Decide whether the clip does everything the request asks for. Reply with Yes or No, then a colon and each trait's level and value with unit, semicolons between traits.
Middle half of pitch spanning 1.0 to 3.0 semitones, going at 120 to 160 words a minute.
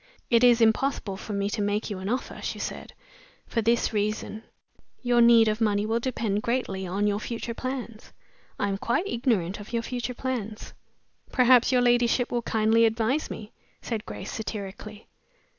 No: narrow, 2.5 semitones; average, 170 wpm